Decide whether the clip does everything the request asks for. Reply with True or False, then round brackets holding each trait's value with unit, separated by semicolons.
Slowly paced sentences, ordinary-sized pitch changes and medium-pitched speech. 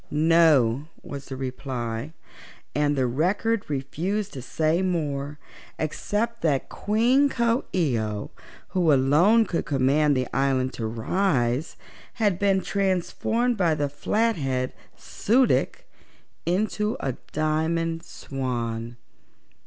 False (115 wpm; 6.8 semitones; 155 Hz)